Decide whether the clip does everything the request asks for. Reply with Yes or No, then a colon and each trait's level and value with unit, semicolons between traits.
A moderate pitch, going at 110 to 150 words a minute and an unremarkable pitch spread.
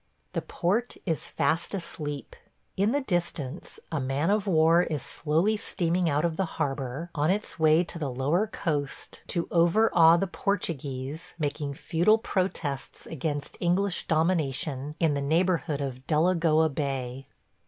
Yes: medium, 160 Hz; average, 145 wpm; average, 3.7 semitones